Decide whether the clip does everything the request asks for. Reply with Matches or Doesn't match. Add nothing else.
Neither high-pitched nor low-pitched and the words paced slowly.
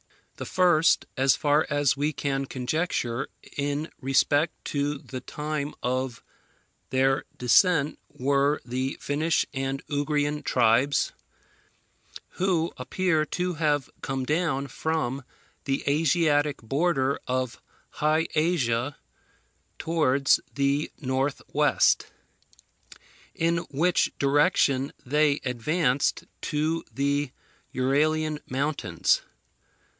Matches